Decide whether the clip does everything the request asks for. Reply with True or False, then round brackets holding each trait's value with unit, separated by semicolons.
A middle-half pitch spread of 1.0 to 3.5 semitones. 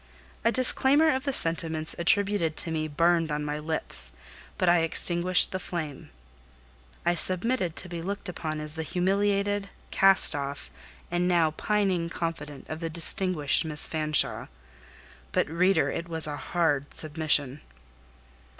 True (3.1 semitones)